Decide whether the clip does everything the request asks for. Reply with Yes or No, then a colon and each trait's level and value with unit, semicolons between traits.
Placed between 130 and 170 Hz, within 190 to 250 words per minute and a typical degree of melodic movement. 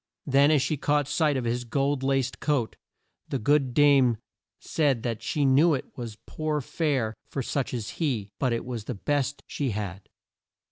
No: low, 135 Hz; average, 180 wpm; average, 3.5 semitones